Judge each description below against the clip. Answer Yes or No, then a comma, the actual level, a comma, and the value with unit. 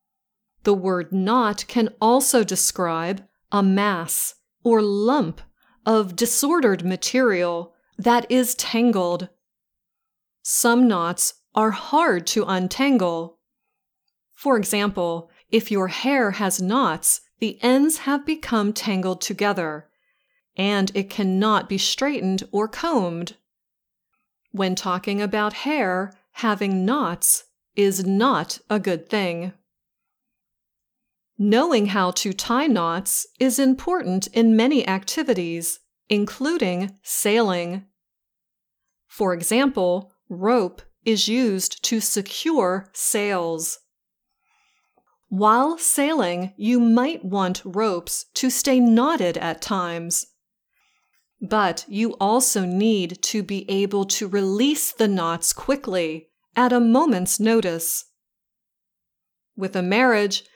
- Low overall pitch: No, high, 205 Hz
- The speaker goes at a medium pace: No, slow, 100 wpm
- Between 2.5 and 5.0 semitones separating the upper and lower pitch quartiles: Yes, average, 4.7 semitones